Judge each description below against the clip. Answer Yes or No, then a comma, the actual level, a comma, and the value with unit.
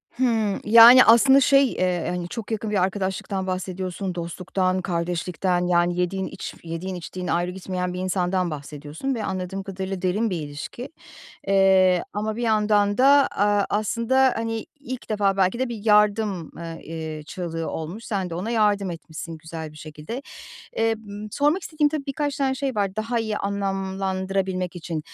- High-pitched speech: Yes, high, 195 Hz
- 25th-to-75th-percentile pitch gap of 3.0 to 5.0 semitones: Yes, average, 3.7 semitones